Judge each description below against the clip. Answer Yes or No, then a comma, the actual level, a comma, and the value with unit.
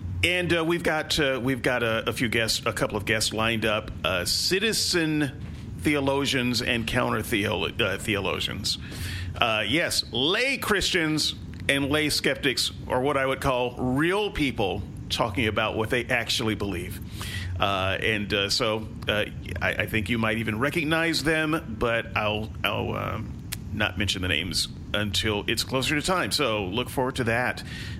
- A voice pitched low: Yes, low, 115 Hz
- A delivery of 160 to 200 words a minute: Yes, average, 165 wpm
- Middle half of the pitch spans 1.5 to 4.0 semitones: No, average, 4.8 semitones